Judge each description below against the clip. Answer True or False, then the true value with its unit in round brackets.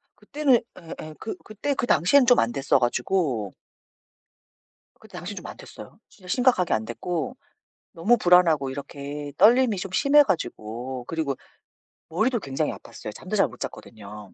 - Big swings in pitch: True (9.0 semitones)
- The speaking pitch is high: False (165 Hz)